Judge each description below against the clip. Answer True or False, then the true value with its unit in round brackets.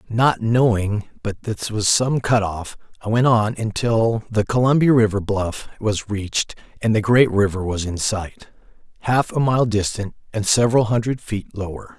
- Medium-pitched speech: False (110 Hz)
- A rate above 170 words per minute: False (165 wpm)